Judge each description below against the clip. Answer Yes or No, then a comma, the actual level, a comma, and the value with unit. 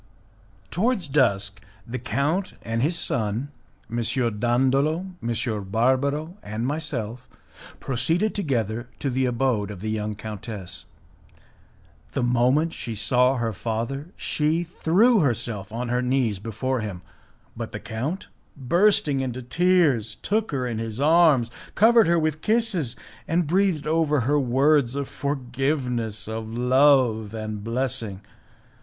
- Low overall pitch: Yes, low, 130 Hz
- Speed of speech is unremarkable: No, slow, 130 wpm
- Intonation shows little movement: No, average, 5.1 semitones